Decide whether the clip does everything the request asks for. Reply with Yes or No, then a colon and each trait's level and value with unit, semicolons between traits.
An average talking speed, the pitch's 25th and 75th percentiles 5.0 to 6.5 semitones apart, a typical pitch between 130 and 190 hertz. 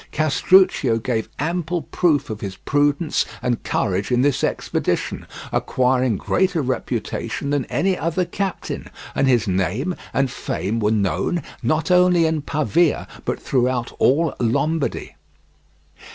No: slow, 125 wpm; wide, 5.5 semitones; medium, 140 Hz